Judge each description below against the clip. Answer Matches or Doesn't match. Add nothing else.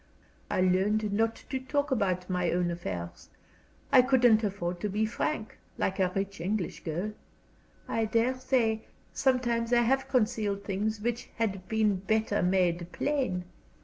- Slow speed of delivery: Doesn't match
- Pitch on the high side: Matches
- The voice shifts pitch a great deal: Doesn't match